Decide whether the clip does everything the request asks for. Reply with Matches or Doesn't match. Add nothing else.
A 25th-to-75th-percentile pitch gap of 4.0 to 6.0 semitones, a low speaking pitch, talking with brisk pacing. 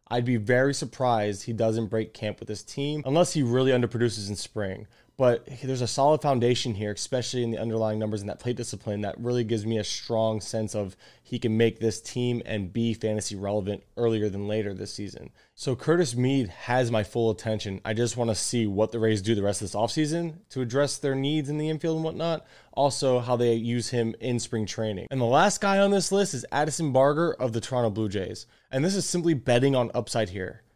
Doesn't match